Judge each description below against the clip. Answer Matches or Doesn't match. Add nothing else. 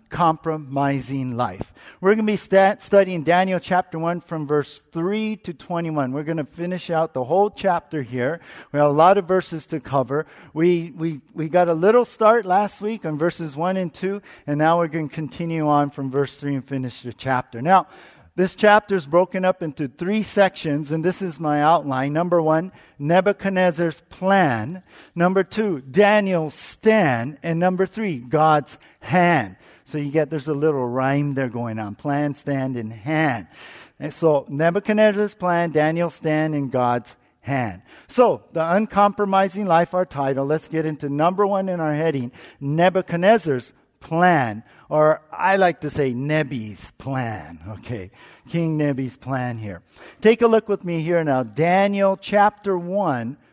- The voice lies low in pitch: Doesn't match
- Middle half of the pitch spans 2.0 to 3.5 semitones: Doesn't match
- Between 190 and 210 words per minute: Doesn't match